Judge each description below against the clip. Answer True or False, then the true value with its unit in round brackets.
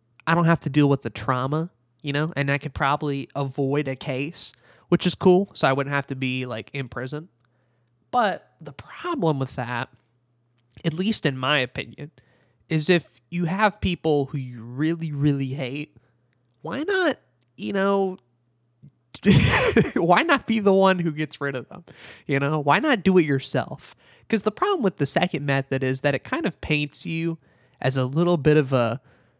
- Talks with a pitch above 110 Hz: True (140 Hz)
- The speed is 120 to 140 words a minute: False (185 wpm)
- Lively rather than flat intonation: False (4.8 semitones)